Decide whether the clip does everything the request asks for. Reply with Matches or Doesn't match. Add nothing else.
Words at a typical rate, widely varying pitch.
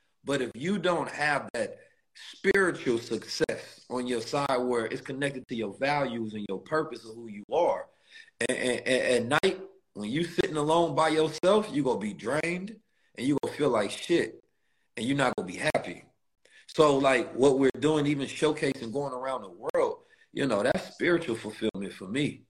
Matches